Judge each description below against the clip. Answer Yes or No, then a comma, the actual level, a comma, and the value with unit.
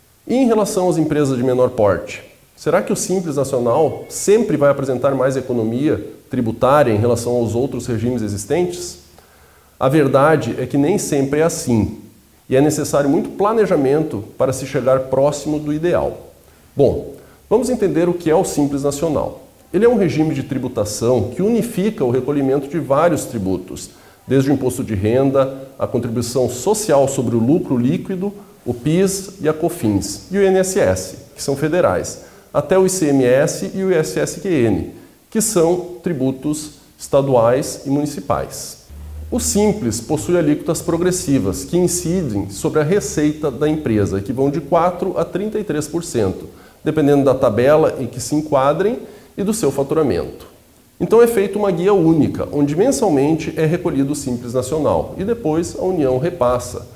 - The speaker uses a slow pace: No, average, 155 wpm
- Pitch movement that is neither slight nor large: No, wide, 5.7 semitones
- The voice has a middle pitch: Yes, medium, 145 Hz